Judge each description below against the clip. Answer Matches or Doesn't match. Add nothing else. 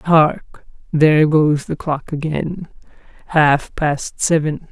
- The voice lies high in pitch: Doesn't match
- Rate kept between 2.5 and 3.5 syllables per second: Matches